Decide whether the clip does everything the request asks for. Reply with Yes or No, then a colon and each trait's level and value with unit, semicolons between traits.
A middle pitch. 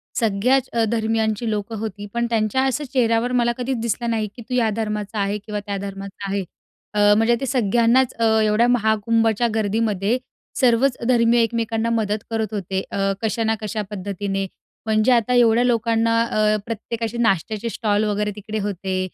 No: high, 225 Hz